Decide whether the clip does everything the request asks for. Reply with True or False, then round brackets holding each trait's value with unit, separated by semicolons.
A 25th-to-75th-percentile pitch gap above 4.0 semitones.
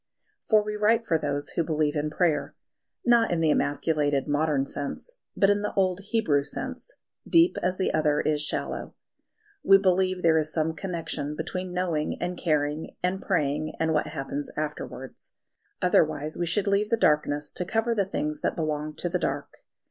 True (4.4 semitones)